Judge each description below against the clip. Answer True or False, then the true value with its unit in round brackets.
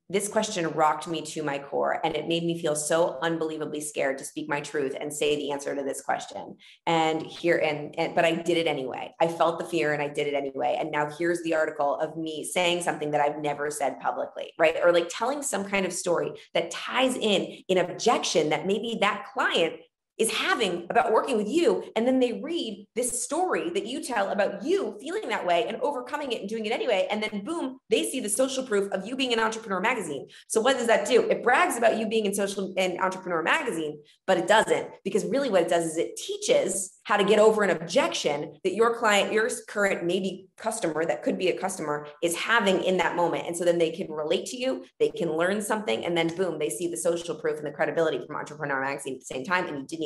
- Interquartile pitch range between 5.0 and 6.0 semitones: True (5.6 semitones)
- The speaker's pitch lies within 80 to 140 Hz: False (180 Hz)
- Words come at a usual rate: False (235 wpm)